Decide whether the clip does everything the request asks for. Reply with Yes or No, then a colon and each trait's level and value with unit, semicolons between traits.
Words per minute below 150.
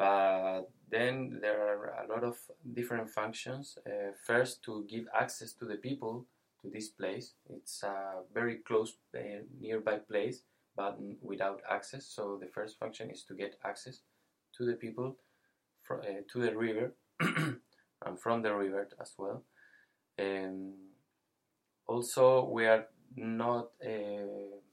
Yes: slow, 135 wpm